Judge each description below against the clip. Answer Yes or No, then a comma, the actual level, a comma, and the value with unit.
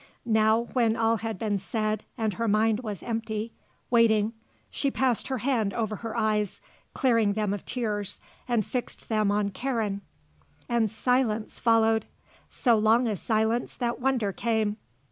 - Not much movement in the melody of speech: Yes, narrow, 1.7 semitones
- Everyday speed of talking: Yes, average, 150 wpm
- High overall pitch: Yes, high, 220 Hz